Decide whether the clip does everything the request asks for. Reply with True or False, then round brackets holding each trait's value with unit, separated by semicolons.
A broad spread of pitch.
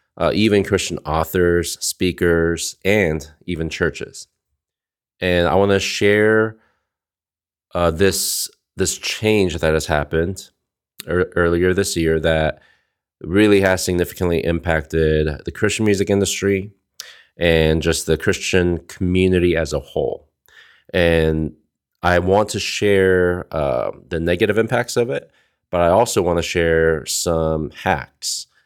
False (3.3 semitones)